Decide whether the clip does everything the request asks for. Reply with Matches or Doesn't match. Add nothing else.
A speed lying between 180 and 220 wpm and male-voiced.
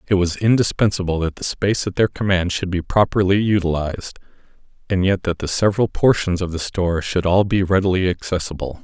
Matches